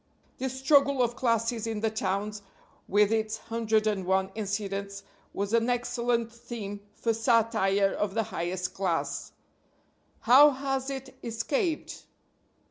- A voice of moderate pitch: No, high, 225 Hz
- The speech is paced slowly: Yes, slow, 130 wpm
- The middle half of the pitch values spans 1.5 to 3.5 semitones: Yes, average, 3.2 semitones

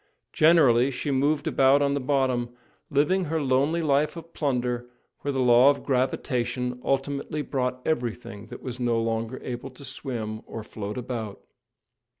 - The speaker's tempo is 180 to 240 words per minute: No, average, 150 wpm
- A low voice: Yes, low, 130 Hz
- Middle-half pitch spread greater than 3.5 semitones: No, average, 2.8 semitones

